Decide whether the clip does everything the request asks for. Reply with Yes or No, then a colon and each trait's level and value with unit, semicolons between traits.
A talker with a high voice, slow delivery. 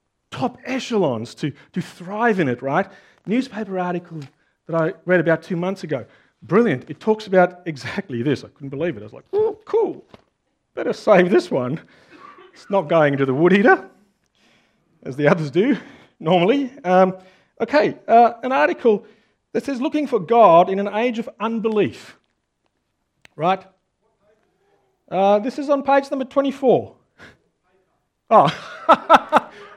No: high, 195 Hz; average, 145 wpm